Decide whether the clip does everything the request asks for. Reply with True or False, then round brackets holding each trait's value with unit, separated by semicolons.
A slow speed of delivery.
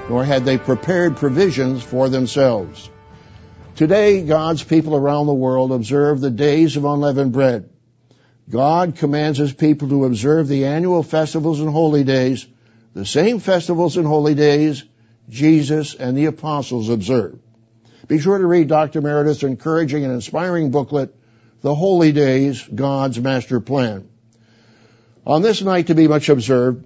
False (145 wpm)